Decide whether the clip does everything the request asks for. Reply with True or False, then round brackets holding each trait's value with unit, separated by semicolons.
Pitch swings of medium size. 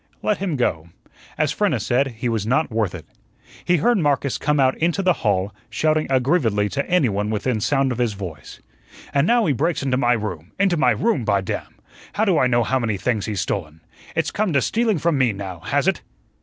False (6.9 semitones)